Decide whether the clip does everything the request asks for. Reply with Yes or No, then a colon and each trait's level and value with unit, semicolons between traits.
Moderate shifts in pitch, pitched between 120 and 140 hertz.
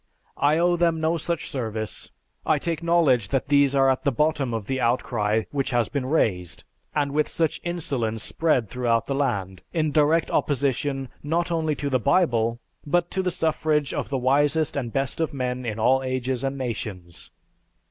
Yes: average, 4.4 semitones; low, 135 Hz